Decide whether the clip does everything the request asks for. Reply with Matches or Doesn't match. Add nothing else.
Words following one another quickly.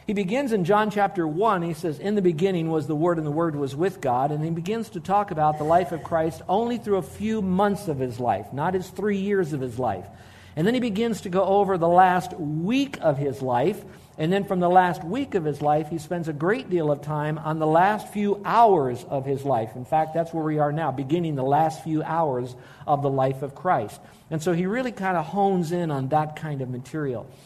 Matches